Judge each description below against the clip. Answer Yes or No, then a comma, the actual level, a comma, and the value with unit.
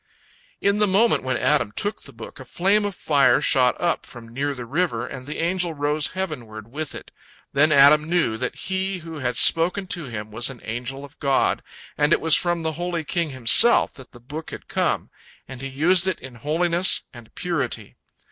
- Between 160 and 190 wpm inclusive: No, average, 200 wpm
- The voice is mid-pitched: Yes, medium, 150 Hz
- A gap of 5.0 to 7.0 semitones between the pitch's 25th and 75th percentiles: Yes, average, 5.3 semitones